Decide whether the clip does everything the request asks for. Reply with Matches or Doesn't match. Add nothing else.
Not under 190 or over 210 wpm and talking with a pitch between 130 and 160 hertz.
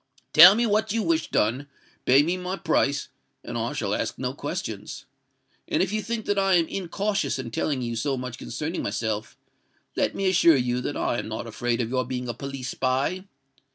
Matches